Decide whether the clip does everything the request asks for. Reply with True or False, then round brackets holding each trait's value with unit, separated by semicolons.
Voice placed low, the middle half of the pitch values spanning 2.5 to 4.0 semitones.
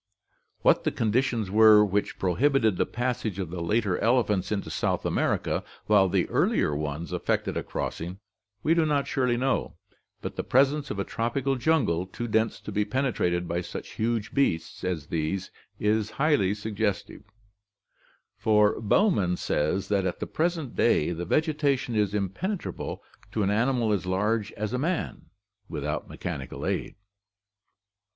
False (105 Hz; 5.4 semitones)